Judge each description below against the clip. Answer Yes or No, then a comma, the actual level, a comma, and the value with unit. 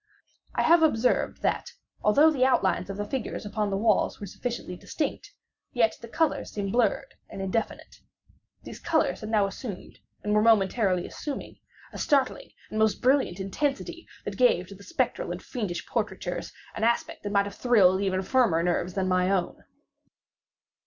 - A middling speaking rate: Yes, average, 165 wpm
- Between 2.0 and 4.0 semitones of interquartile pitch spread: No, average, 5.0 semitones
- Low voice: No, high, 215 Hz